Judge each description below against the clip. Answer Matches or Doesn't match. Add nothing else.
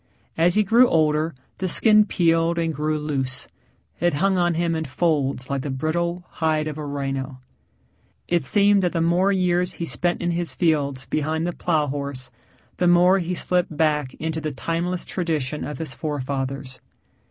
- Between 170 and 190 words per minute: Matches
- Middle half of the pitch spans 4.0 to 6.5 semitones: Doesn't match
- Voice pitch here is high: Doesn't match